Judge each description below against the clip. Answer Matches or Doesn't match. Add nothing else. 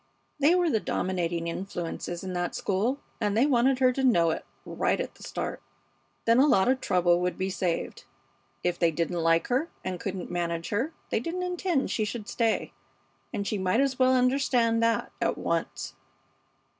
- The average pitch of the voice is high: Matches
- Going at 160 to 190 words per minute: Matches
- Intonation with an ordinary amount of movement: Doesn't match